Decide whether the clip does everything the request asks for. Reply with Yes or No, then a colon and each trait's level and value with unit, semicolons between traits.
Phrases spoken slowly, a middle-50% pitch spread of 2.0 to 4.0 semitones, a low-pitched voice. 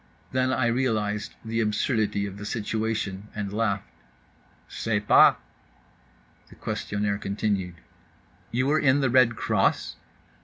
Yes: slow, 115 wpm; average, 2.7 semitones; low, 105 Hz